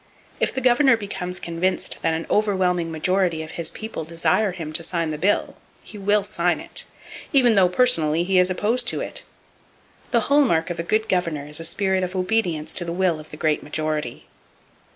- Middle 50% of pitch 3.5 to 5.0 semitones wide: Yes, average, 4.1 semitones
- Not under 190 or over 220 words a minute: Yes, average, 195 wpm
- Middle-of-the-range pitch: Yes, medium, 180 Hz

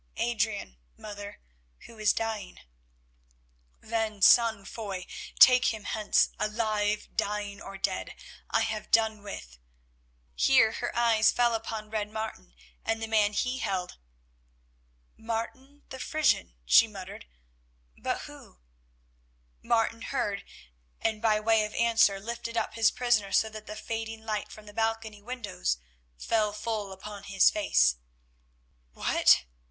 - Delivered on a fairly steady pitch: Yes, narrow, 1.8 semitones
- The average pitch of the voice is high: Yes, high, 215 Hz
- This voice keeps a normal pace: No, slow, 130 wpm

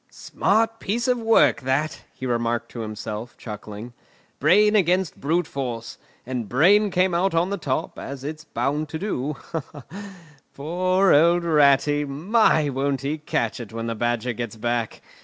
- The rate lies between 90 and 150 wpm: Yes, average, 145 wpm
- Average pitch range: No, wide, 6.9 semitones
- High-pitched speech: No, medium, 145 Hz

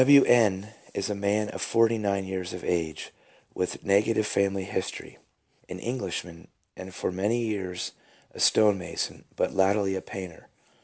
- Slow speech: No, average, 150 wpm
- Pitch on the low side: Yes, low, 100 Hz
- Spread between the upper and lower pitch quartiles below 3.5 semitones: Yes, narrow, 2.4 semitones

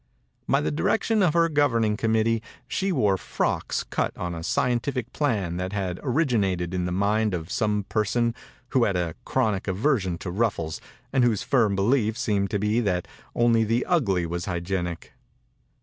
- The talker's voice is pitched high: No, low, 105 Hz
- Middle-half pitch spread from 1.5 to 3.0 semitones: No, average, 4.7 semitones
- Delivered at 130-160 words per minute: No, average, 180 wpm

